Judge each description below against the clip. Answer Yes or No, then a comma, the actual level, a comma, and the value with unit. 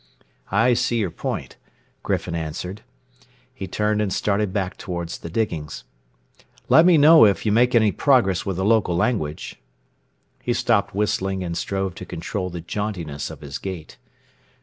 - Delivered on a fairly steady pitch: No, average, 4.1 semitones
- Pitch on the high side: No, very low, 95 Hz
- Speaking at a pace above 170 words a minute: No, average, 155 wpm